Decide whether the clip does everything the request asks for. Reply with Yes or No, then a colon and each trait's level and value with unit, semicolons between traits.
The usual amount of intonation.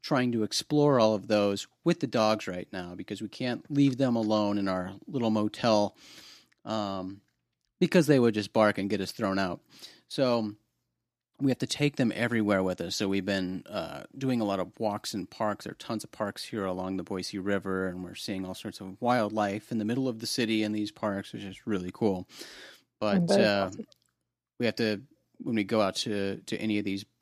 Yes: average, 3.3 semitones